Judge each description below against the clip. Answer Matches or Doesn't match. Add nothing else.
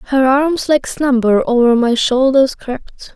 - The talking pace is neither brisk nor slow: Matches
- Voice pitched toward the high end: Matches